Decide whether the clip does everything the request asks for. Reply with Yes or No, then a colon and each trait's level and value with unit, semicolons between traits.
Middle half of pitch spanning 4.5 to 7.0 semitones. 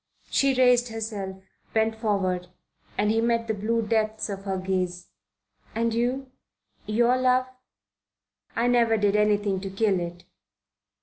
No: average, 3.1 semitones